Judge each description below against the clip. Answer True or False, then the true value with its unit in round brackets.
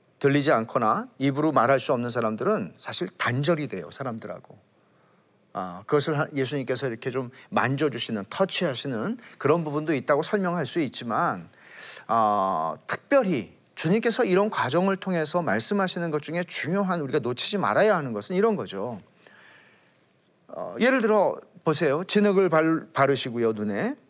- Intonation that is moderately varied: False (5.8 semitones)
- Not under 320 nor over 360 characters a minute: True (325 characters per minute)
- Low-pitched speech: False (155 Hz)